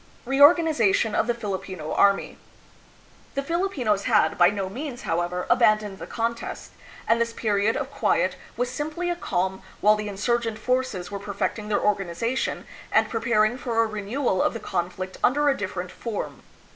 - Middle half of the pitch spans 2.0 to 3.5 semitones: No, average, 4.0 semitones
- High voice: Yes, high, 220 Hz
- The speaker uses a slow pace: No, average, 165 wpm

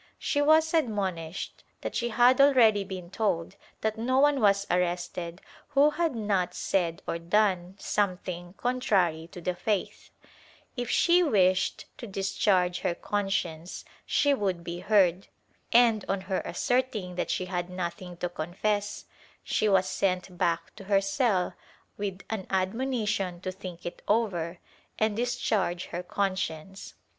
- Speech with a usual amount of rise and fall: Yes, average, 3.6 semitones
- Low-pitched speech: No, high, 195 Hz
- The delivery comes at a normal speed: Yes, average, 145 wpm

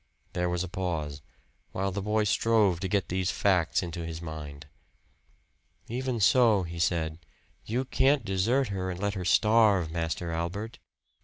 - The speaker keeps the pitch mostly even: No, average, 4.1 semitones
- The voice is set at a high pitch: No, very low, 95 Hz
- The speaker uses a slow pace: No, average, 155 wpm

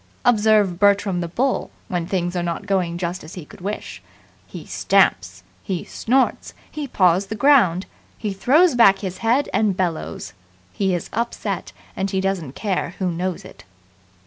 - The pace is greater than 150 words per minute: Yes, average, 165 wpm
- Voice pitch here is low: No, high, 195 Hz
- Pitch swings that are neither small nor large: Yes, average, 3.6 semitones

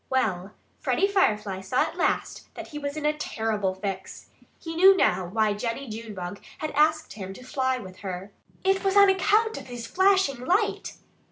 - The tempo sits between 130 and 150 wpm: No, average, 180 wpm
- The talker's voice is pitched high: Yes, very high, 255 Hz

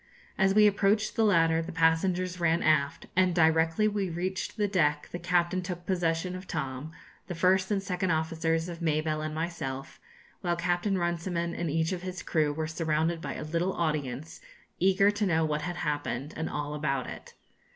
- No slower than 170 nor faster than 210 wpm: Yes, average, 185 wpm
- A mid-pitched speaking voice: Yes, medium, 170 Hz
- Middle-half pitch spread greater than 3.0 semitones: No, average, 2.7 semitones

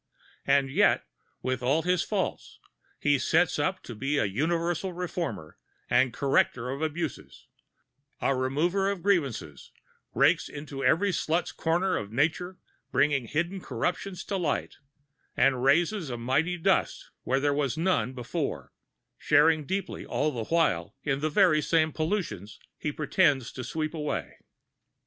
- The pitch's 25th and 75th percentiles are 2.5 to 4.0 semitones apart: No, average, 4.7 semitones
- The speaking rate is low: No, average, 145 wpm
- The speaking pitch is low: No, medium, 150 Hz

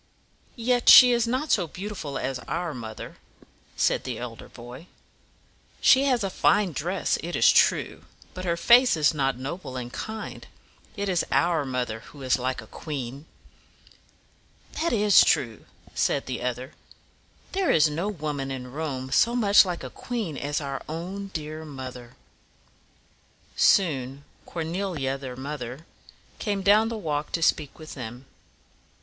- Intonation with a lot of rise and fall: Yes, wide, 6.9 semitones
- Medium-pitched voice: Yes, medium, 155 Hz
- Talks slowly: No, average, 155 wpm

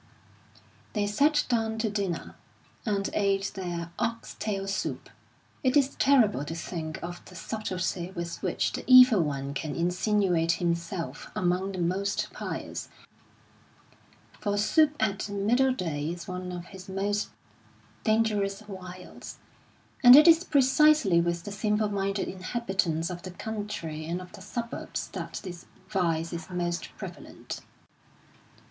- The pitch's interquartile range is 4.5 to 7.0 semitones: No, average, 3.9 semitones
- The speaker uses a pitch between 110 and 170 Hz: No, high, 195 Hz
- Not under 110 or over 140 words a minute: Yes, slow, 135 wpm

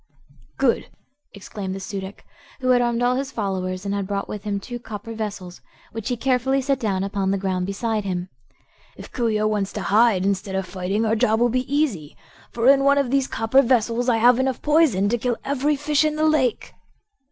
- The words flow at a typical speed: No, fast, 215 wpm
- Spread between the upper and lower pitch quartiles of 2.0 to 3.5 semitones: No, average, 4.6 semitones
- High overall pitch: Yes, high, 225 Hz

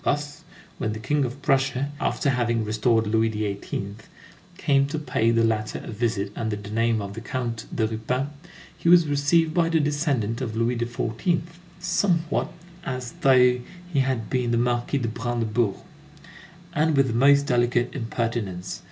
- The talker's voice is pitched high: No, low, 120 Hz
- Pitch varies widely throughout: No, average, 4.0 semitones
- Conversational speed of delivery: Yes, average, 160 wpm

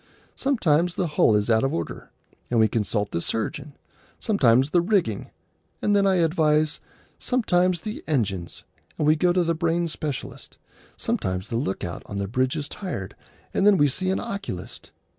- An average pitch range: No, wide, 8.1 semitones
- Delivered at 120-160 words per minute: No, average, 175 wpm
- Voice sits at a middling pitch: Yes, medium, 150 Hz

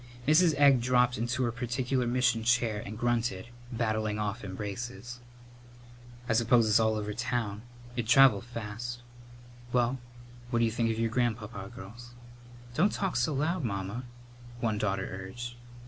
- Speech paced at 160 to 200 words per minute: No, average, 145 wpm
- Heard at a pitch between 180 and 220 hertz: No, low, 120 Hz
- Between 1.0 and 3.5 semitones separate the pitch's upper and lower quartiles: Yes, narrow, 2.4 semitones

